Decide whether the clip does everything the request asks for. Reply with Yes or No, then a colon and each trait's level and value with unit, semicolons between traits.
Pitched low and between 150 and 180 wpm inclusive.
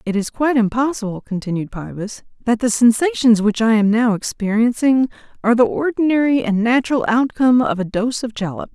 No: high, 230 Hz; average, 170 wpm